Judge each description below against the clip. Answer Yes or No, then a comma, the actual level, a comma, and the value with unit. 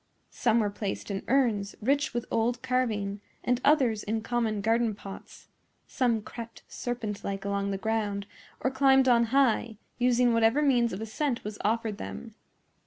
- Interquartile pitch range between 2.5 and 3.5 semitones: Yes, average, 3.0 semitones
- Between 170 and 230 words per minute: No, average, 160 wpm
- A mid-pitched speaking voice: No, high, 230 Hz